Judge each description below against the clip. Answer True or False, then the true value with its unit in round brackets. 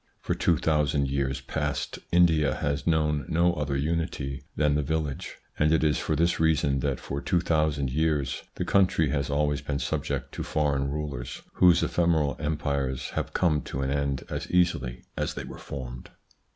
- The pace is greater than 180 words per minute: False (175 wpm)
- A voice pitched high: False (75 Hz)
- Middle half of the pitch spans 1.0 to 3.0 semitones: True (2.4 semitones)